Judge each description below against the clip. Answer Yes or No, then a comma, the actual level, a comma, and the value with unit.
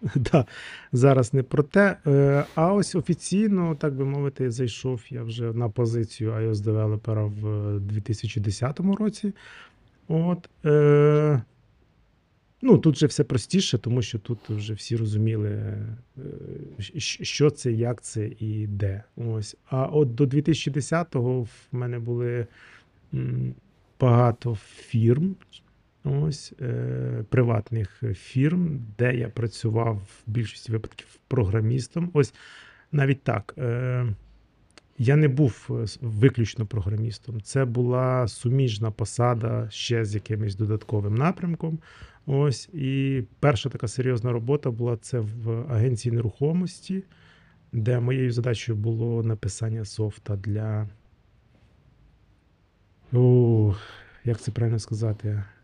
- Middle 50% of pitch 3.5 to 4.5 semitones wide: Yes, average, 3.9 semitones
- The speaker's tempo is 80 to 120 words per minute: Yes, average, 110 wpm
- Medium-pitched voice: No, low, 120 Hz